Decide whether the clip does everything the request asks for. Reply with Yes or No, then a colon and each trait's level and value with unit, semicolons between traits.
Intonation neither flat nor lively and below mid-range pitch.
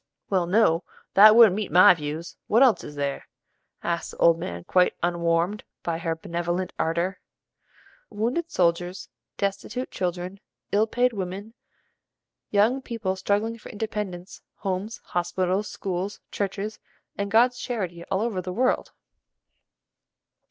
No: average, 3.7 semitones; high, 190 Hz